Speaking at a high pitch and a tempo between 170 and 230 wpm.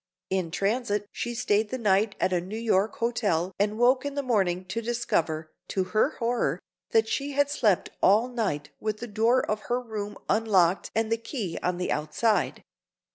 Yes: high, 215 Hz; average, 185 wpm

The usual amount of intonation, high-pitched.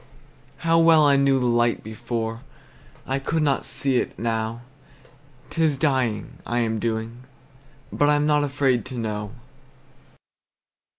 No: average, 4.1 semitones; low, 125 Hz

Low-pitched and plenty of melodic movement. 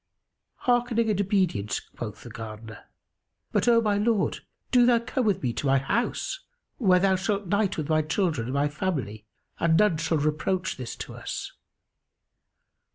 No: medium, 180 Hz; wide, 7.5 semitones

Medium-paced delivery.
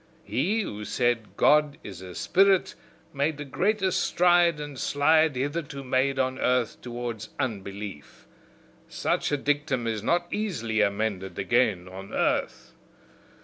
No: slow, 130 wpm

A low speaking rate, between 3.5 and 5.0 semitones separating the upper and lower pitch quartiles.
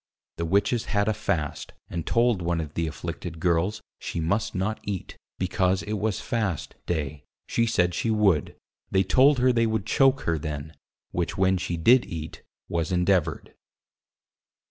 No: average, 165 wpm; average, 4.6 semitones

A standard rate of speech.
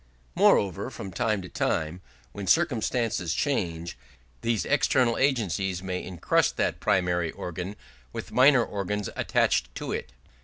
No: slow, 125 wpm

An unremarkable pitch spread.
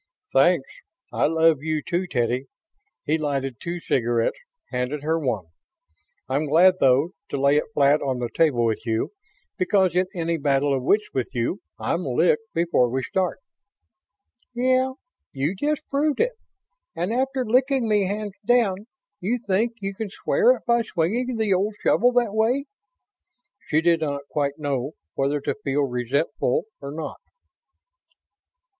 No: wide, 7.7 semitones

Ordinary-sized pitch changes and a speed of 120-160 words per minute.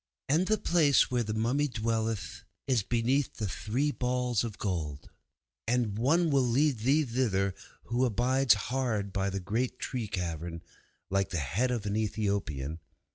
Yes: average, 4.5 semitones; average, 155 wpm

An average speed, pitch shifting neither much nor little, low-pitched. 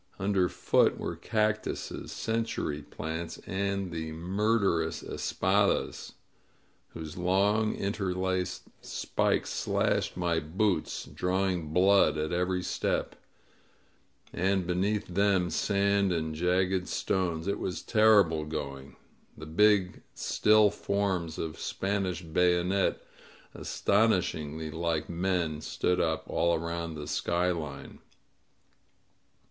No: slow, 100 wpm; average, 3.3 semitones; very low, 90 Hz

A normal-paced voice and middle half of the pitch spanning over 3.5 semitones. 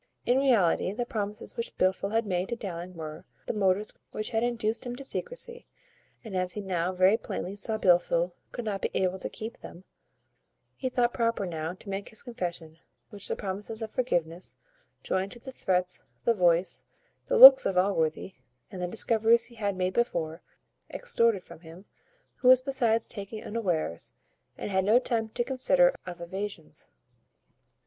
Yes: average, 170 wpm; average, 4.4 semitones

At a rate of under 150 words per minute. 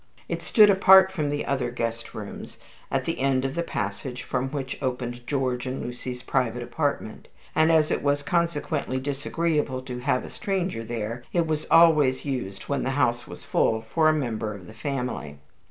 No: average, 185 wpm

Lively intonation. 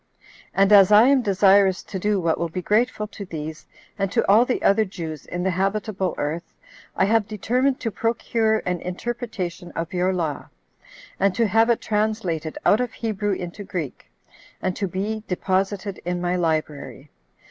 No: average, 3.4 semitones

